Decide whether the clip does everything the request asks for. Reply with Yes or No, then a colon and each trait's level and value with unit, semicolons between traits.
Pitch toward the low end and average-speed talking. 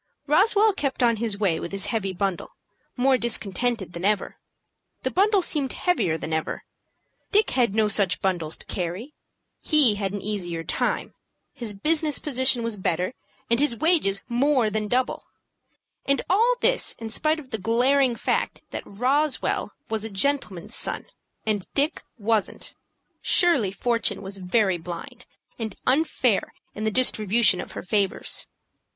No: high, 225 Hz; average, 150 wpm